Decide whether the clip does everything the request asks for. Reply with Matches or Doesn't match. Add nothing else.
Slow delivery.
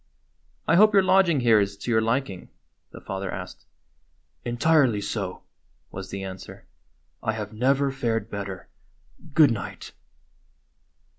Matches